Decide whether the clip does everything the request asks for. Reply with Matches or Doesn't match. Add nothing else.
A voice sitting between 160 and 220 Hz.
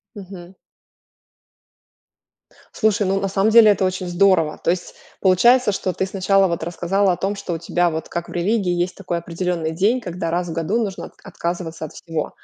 Matches